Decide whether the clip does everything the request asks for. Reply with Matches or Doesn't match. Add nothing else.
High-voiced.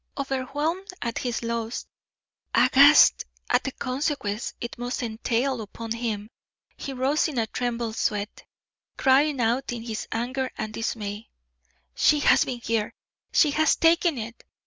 Matches